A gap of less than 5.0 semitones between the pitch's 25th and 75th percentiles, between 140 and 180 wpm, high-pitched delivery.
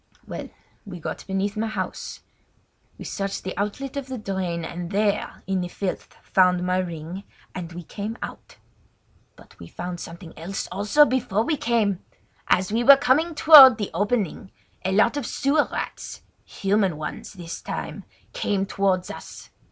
Yes: average, 4.3 semitones; average, 155 wpm; high, 195 Hz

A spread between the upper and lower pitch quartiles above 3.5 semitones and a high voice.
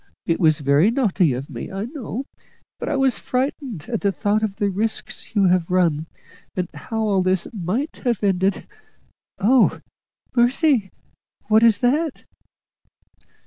Yes: average, 5.0 semitones; high, 205 Hz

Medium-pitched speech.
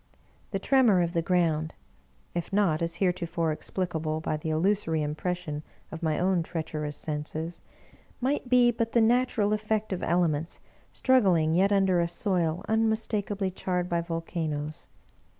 Yes: medium, 175 Hz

